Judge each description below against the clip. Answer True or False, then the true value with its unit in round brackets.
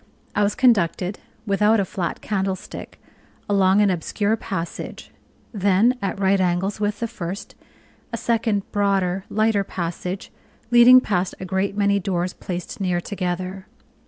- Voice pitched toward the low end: False (195 Hz)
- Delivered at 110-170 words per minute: True (135 wpm)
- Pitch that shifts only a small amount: True (2.1 semitones)